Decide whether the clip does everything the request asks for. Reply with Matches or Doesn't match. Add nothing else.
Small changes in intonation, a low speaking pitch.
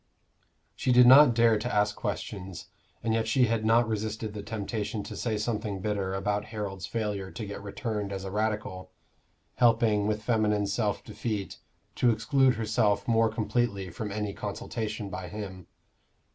Matches